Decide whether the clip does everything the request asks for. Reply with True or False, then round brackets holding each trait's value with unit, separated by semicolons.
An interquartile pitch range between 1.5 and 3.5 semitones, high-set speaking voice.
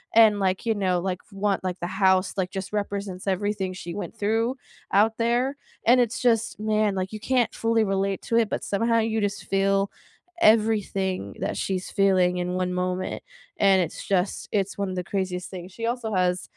True (2.9 semitones; 195 Hz)